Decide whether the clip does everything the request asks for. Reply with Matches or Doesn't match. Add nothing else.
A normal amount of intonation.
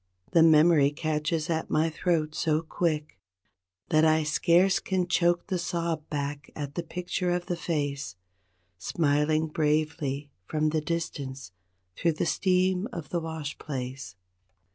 Doesn't match